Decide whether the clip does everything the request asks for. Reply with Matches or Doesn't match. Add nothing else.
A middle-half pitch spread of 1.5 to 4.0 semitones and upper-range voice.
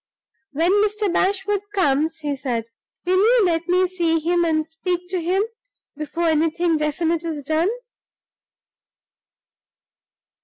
Matches